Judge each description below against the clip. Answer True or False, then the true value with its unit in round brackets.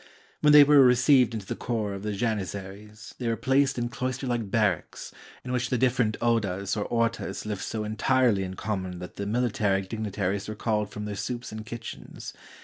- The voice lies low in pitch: True (110 Hz)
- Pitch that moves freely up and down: False (3.3 semitones)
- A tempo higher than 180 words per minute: True (200 wpm)